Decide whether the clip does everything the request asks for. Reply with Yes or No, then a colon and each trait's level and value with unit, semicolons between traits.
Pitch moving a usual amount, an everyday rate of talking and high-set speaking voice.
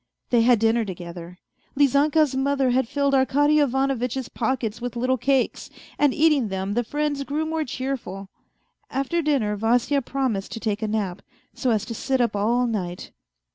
Yes: average, 4.1 semitones; average, 165 wpm; very high, 250 Hz